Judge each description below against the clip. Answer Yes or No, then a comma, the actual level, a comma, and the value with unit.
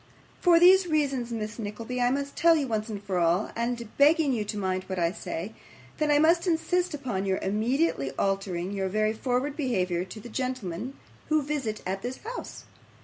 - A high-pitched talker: Yes, high, 235 Hz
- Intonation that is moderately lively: No, wide, 6.9 semitones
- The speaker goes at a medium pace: Yes, average, 185 wpm